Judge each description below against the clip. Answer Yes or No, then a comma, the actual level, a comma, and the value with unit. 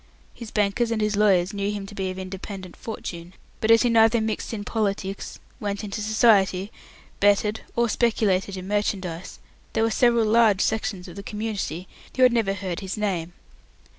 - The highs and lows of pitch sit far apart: No, narrow, 2.5 semitones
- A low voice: No, high, 205 Hz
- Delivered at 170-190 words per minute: Yes, average, 175 wpm